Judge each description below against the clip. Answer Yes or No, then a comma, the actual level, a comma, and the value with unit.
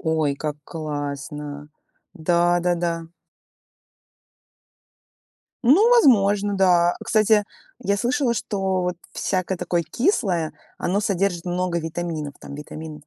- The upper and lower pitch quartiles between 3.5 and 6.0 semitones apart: Yes, average, 4.0 semitones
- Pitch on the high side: No, medium, 175 Hz